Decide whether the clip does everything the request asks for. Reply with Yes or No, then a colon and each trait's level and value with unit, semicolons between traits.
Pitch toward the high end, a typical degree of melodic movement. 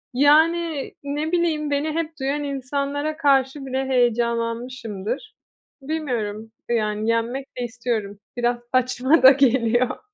Yes: very high, 265 Hz; average, 3.6 semitones